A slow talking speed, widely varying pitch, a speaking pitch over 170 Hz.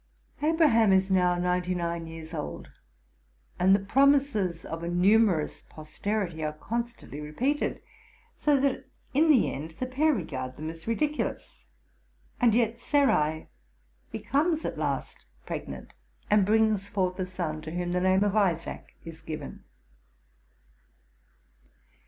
Yes: slow, 130 wpm; wide, 6.3 semitones; high, 190 Hz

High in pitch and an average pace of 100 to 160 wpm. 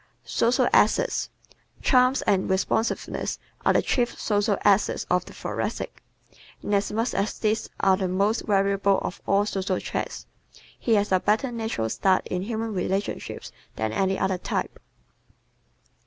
Yes: high, 200 Hz; average, 140 wpm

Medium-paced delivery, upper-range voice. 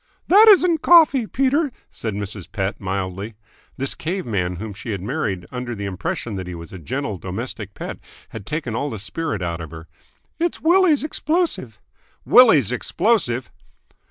No: average, 160 wpm; low, 120 Hz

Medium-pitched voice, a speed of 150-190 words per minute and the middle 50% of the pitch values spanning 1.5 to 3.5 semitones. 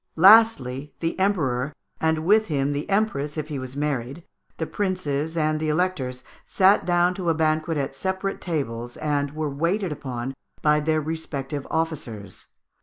No: medium, 155 Hz; average, 155 wpm; average, 3.9 semitones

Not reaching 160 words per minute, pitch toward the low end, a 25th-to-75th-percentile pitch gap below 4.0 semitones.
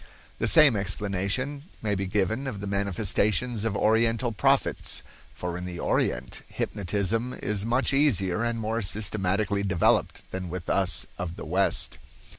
Yes: average, 140 wpm; low, 100 Hz; average, 3.1 semitones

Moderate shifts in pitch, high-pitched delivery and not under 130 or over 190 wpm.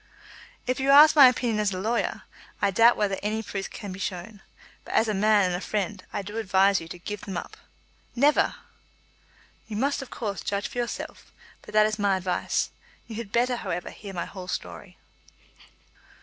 No: average, 3.3 semitones; high, 210 Hz; average, 200 wpm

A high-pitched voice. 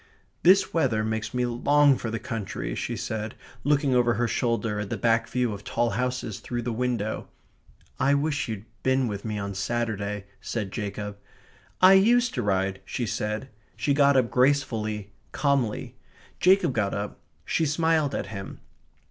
No: low, 120 Hz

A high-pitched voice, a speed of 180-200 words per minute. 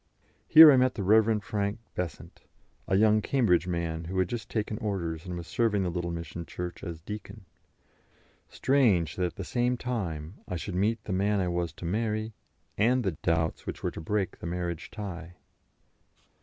No: very low, 95 Hz; average, 185 wpm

